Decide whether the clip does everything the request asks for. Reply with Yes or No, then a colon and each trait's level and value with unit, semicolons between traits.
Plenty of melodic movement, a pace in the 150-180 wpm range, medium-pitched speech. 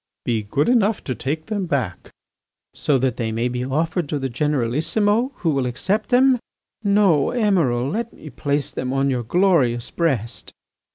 Yes: wide, 7.8 semitones; average, 165 wpm; medium, 145 Hz